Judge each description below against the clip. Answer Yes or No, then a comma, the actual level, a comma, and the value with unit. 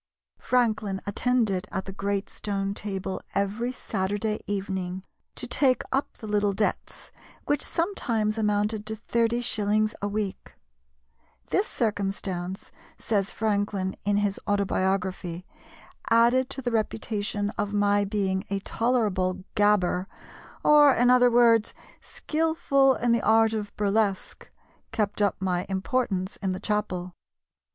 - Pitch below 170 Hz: No, high, 205 Hz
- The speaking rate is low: Yes, slow, 125 wpm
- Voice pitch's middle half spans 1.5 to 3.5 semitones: Yes, average, 2.8 semitones